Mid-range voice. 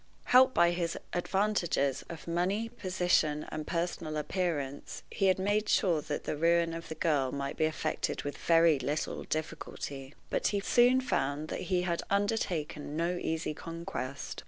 Yes: medium, 165 Hz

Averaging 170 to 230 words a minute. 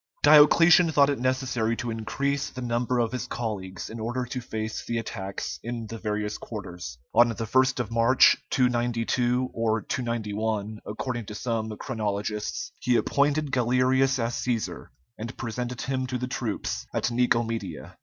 No: average, 155 wpm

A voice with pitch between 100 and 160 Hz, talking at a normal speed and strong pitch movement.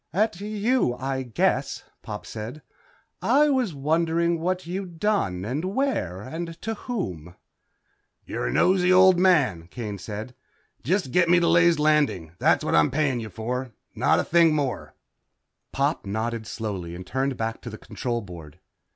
Yes: medium, 140 Hz; average, 155 wpm; wide, 8.5 semitones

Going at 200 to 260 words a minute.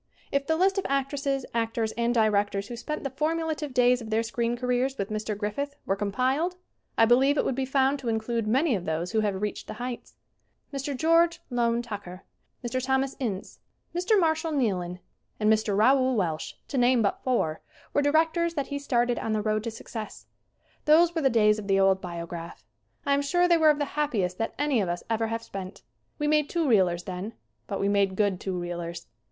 Yes: fast, 205 wpm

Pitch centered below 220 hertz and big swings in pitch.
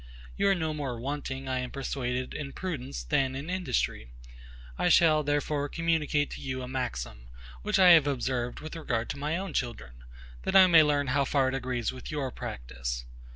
No: low, 135 Hz; average, 3.6 semitones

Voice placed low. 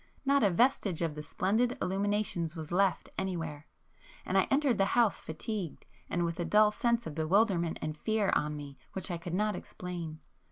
No: medium, 185 Hz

